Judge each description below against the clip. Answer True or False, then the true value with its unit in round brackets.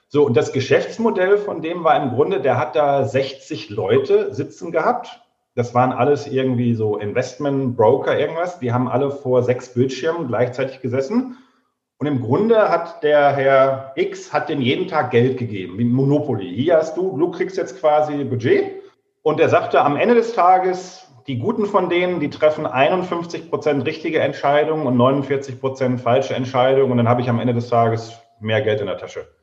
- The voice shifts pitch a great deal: True (6.6 semitones)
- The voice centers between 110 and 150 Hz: True (140 Hz)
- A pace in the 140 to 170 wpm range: False (180 wpm)